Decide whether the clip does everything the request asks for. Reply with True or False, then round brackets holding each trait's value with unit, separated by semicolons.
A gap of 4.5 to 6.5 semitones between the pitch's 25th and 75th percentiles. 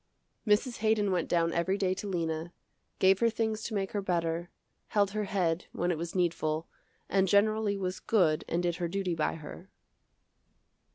False (3.3 semitones)